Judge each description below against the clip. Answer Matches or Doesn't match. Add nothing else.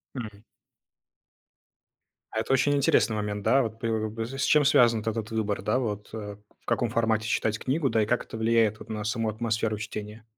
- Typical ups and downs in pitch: Doesn't match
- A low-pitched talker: Matches